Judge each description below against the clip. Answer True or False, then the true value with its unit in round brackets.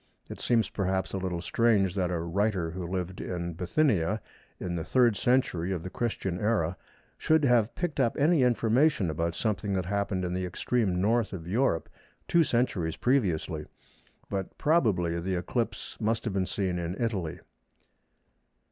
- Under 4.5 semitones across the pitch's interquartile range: False (5.0 semitones)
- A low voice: True (95 Hz)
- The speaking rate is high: False (160 wpm)